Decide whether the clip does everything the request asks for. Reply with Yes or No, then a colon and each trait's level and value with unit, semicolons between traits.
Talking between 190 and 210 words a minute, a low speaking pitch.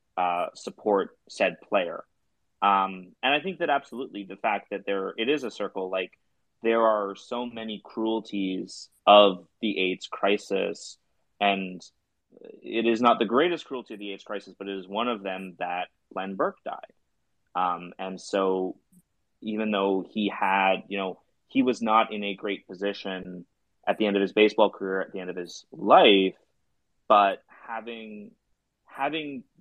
No: average, 165 wpm; low, 100 Hz